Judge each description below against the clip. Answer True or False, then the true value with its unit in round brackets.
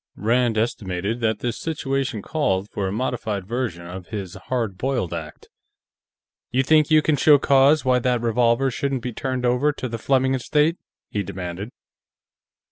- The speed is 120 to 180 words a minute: True (160 wpm)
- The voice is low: True (120 Hz)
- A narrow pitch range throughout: False (4.5 semitones)